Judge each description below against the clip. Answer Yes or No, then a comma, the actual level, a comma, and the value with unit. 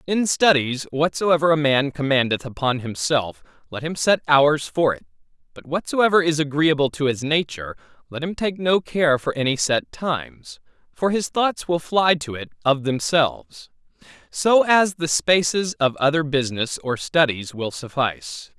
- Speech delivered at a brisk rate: No, average, 160 wpm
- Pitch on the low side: No, medium, 145 Hz